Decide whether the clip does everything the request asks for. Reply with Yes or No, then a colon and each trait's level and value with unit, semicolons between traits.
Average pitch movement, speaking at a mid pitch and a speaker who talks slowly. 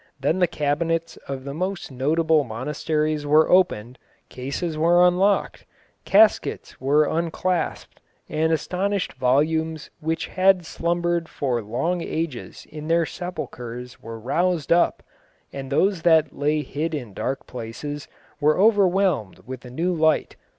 Yes: average, 4.0 semitones; medium, 155 Hz; slow, 130 wpm